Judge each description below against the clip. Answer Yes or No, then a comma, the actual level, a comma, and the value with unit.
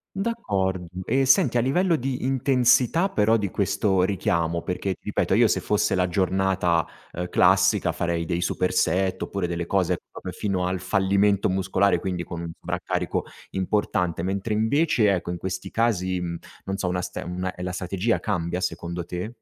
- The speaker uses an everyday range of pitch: Yes, average, 3.0 semitones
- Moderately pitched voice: No, very low, 95 Hz